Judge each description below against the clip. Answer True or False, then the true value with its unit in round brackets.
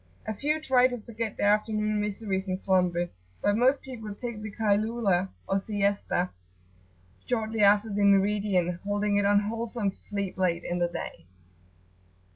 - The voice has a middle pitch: False (205 Hz)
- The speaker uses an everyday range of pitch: False (2.3 semitones)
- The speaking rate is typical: True (150 wpm)